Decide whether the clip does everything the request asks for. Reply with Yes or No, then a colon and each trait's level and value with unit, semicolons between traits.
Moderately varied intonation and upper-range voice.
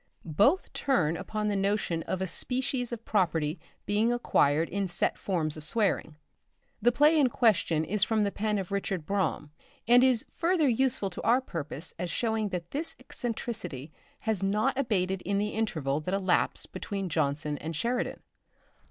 No: wide, 5.8 semitones; high, 200 Hz